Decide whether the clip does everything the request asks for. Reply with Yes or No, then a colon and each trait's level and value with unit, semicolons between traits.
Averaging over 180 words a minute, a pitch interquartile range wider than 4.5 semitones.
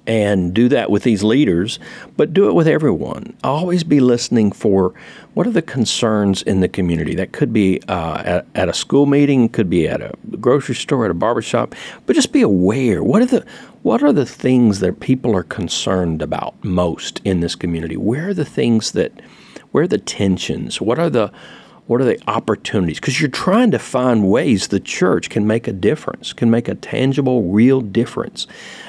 Yes: average, 195 wpm; average, 5.1 semitones